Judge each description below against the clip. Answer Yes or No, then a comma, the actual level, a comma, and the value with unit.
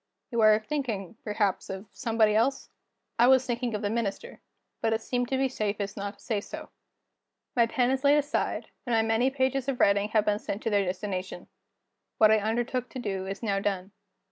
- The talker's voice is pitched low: No, high, 220 Hz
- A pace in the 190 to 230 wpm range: Yes, average, 200 wpm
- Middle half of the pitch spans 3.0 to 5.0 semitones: Yes, average, 3.5 semitones